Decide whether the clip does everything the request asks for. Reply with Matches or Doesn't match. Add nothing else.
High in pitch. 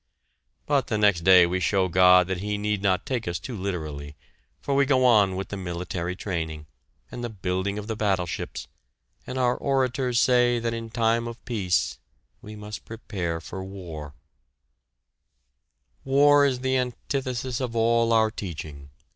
Doesn't match